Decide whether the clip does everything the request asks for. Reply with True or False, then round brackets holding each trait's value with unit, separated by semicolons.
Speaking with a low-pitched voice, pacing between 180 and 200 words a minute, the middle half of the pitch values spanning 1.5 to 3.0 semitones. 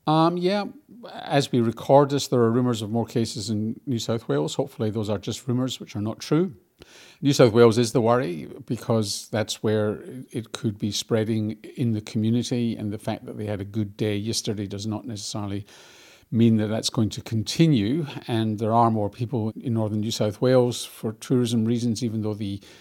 True (115 Hz; 195 wpm; 2.5 semitones)